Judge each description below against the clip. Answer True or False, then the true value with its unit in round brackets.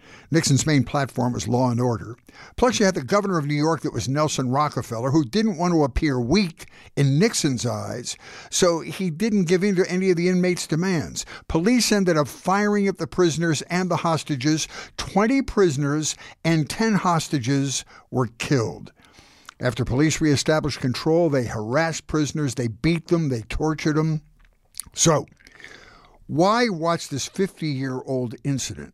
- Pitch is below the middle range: False (155 Hz)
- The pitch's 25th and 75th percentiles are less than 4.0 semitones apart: False (4.9 semitones)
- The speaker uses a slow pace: False (160 wpm)